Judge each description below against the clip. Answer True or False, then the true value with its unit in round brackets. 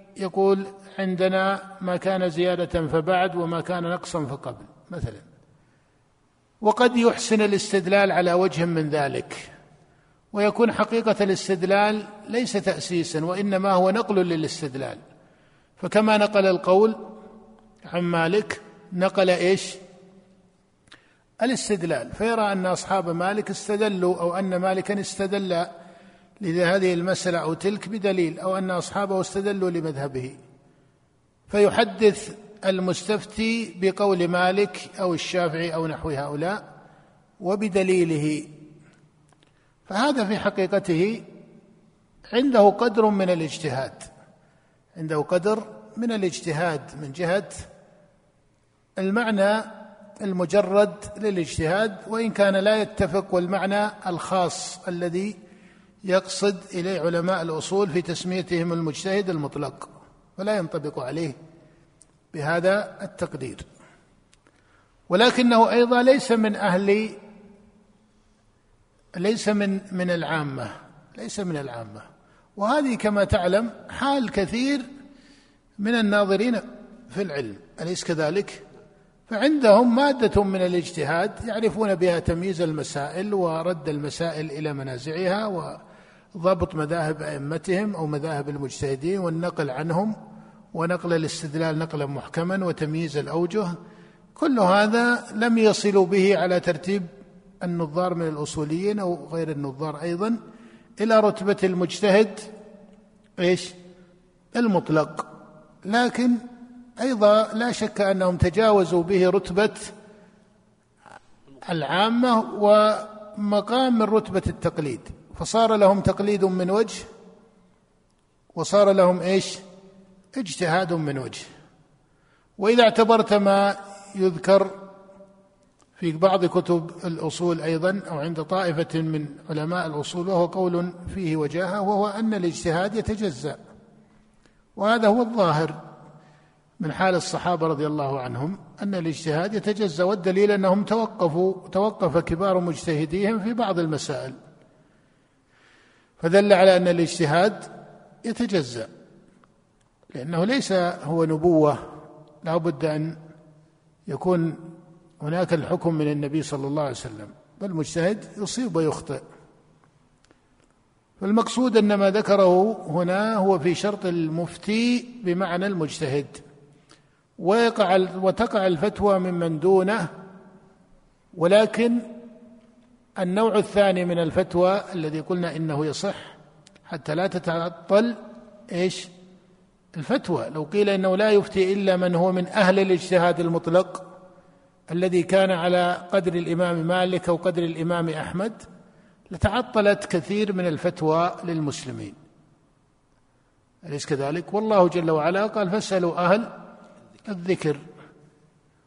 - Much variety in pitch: False (3.7 semitones)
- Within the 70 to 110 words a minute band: True (100 wpm)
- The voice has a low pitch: False (185 Hz)